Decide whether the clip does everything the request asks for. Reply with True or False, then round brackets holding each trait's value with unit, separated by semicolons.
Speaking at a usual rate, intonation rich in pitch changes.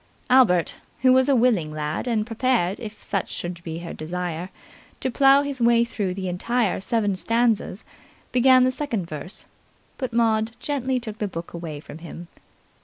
True (170 wpm; 6.1 semitones)